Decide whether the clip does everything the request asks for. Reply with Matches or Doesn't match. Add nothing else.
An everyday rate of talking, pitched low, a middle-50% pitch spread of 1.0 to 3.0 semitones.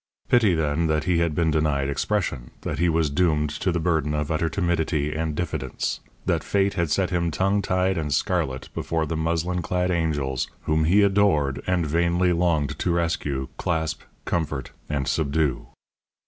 Matches